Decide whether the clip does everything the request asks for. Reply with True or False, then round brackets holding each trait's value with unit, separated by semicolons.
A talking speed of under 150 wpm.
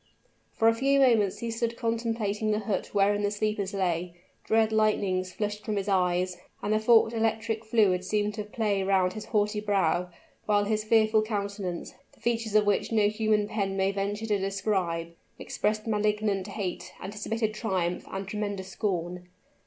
False (165 wpm)